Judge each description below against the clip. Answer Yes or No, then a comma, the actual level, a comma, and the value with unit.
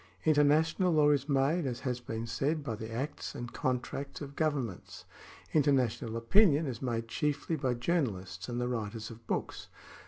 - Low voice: Yes, low, 130 Hz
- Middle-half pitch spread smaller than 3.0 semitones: No, average, 4.2 semitones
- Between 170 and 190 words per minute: Yes, average, 175 wpm